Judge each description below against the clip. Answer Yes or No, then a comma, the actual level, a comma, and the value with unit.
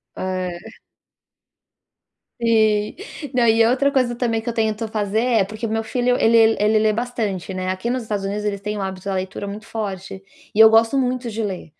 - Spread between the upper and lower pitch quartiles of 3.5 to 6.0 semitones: No, narrow, 2.6 semitones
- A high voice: Yes, high, 220 Hz